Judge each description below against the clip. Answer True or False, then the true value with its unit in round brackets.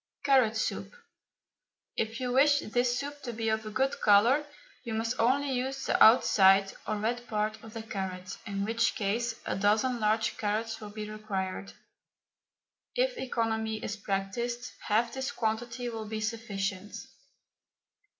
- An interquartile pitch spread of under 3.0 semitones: True (2.4 semitones)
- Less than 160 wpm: True (150 wpm)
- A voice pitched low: False (225 Hz)